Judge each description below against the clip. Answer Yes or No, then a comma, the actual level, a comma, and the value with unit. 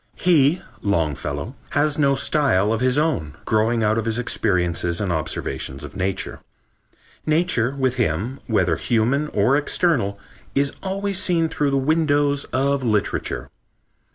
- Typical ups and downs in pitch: No, wide, 6.6 semitones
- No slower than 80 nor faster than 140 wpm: Yes, slow, 135 wpm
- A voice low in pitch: Yes, low, 125 Hz